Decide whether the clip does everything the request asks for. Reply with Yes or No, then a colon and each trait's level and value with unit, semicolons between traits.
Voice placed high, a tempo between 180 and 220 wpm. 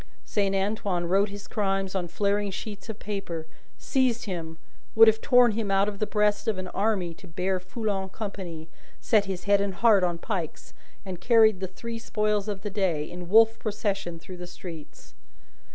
Yes: high, 195 Hz; average, 185 wpm